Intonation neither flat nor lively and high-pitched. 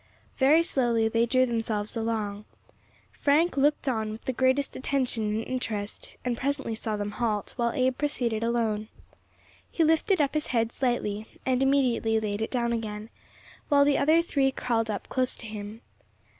Yes: average, 3.6 semitones; high, 235 Hz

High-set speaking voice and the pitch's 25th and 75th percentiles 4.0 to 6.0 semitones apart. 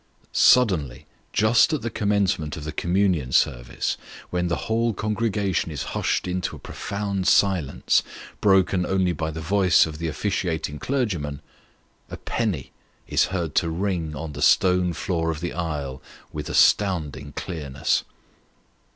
No: very low, 90 Hz; average, 4.5 semitones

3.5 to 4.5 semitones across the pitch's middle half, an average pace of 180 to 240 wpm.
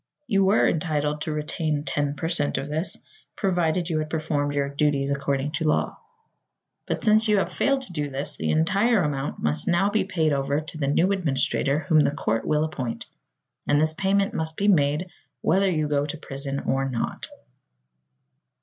Yes: average, 3.8 semitones; average, 185 wpm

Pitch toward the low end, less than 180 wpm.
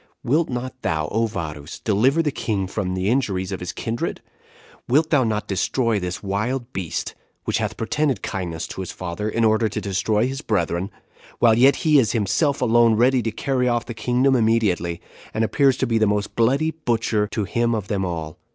No: low, 110 Hz; average, 195 wpm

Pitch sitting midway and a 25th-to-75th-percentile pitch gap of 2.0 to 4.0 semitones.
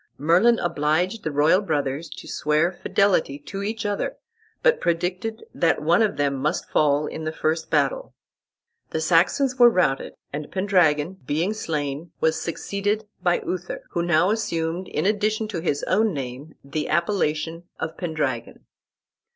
No: medium, 170 Hz; average, 4.7 semitones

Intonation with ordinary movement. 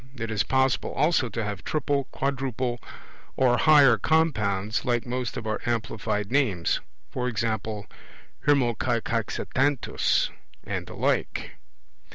Yes: average, 3.6 semitones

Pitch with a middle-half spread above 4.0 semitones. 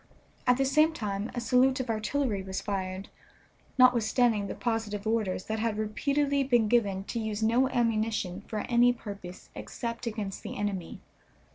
No: average, 3.2 semitones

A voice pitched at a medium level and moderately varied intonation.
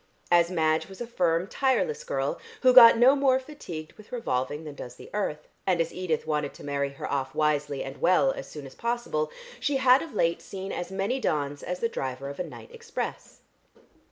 No: medium, 175 Hz; wide, 8.5 semitones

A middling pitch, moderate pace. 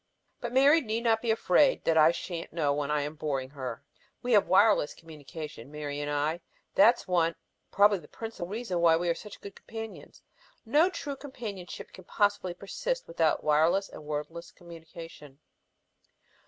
Yes: medium, 170 Hz; average, 165 wpm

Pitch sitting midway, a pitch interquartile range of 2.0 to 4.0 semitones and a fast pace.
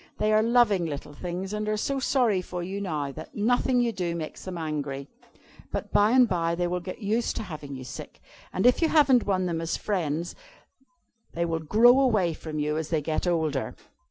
No: medium, 180 Hz; average, 5.2 semitones; fast, 210 wpm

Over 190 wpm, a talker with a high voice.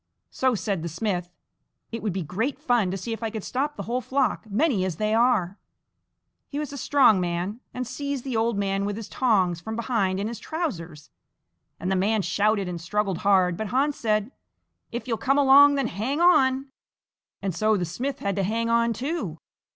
Yes: average, 200 wpm; high, 220 Hz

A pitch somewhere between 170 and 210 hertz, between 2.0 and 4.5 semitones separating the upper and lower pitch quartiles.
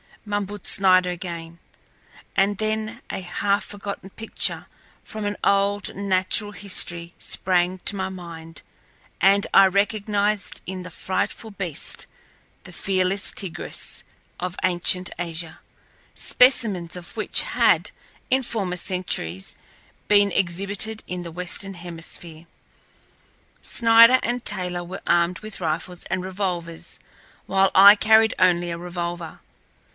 Yes: medium, 185 Hz; narrow, 2.6 semitones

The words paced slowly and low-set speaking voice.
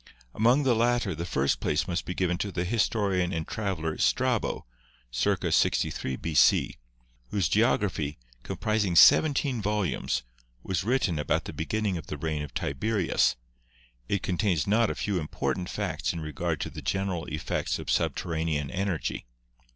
No: average, 160 wpm; very low, 90 Hz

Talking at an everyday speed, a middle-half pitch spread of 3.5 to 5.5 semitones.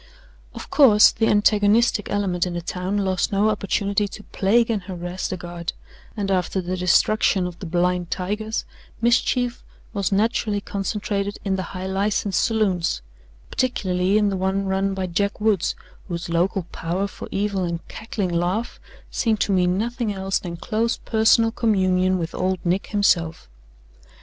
No: average, 155 wpm; narrow, 2.5 semitones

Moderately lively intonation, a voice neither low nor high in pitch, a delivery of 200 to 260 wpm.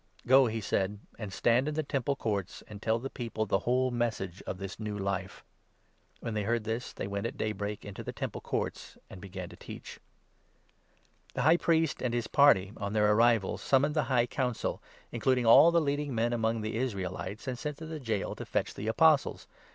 No: average, 4.2 semitones; low, 115 Hz; fast, 205 wpm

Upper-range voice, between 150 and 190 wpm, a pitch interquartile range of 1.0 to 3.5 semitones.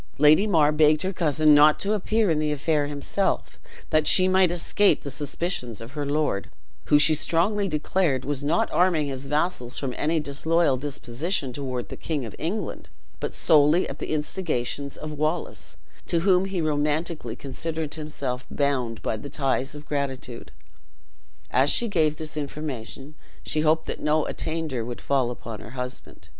No: medium, 150 Hz; average, 165 wpm; average, 3.1 semitones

